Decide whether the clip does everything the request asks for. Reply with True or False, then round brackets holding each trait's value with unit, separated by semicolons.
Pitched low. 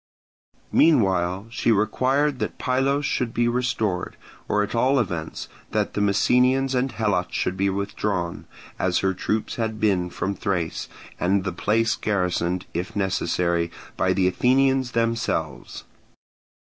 True (105 Hz)